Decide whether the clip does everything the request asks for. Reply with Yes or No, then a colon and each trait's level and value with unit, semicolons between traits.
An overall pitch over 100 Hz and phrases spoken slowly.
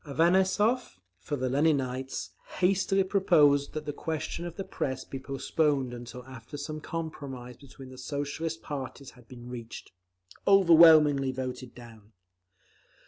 Yes: medium, 140 Hz; slow, 130 wpm